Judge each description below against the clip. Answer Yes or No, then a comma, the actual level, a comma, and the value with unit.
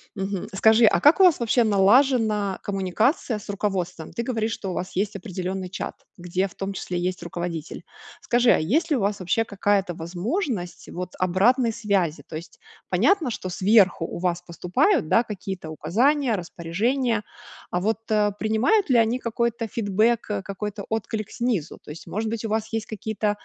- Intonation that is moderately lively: Yes, average, 4.0 semitones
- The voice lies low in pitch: No, high, 205 Hz